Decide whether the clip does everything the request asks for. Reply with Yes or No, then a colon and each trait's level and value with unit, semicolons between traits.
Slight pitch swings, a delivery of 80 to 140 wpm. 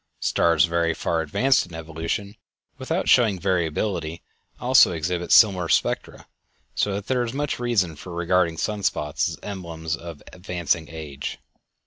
No: average, 3.7 semitones; slow, 135 wpm